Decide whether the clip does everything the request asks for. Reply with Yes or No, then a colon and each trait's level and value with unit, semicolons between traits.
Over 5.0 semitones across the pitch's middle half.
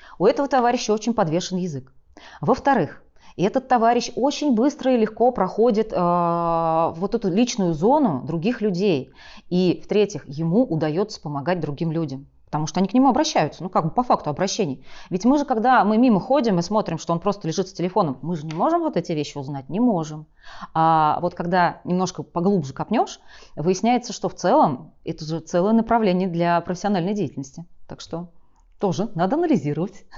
Yes: wide, 5.5 semitones